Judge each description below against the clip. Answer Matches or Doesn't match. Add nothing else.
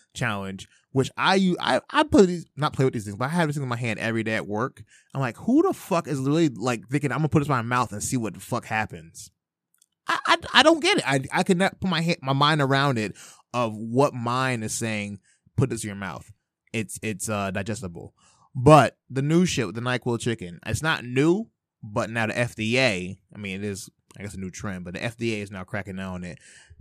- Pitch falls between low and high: Doesn't match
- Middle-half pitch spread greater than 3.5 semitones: Matches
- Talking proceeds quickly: Matches